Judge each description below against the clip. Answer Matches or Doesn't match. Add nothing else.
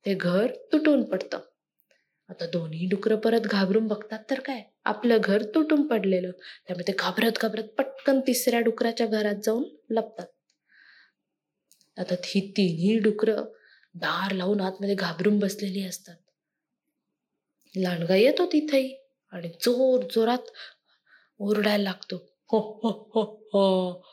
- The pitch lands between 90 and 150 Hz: Doesn't match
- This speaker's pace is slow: Doesn't match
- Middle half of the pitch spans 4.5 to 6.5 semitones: Doesn't match